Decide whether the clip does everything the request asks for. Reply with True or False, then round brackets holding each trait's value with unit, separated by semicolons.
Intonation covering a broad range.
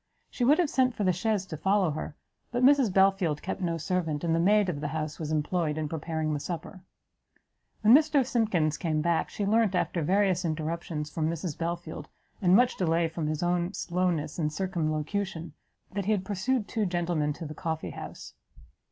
False (4.1 semitones)